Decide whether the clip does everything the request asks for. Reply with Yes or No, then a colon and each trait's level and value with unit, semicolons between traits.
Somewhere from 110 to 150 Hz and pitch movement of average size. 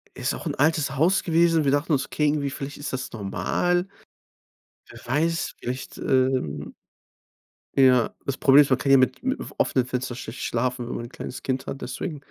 Yes: low, 135 Hz; average, 3.1 semitones